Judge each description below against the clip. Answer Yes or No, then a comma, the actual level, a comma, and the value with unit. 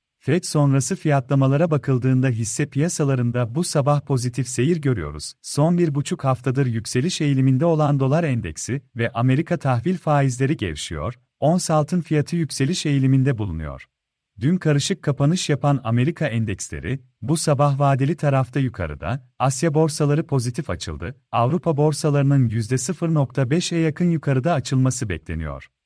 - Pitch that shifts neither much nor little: Yes, average, 3.8 semitones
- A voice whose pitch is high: No, medium, 140 Hz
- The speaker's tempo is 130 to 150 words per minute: No, average, 120 wpm